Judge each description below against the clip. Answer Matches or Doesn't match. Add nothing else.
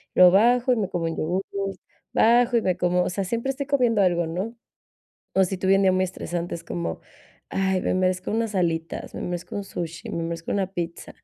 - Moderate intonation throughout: Matches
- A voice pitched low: Doesn't match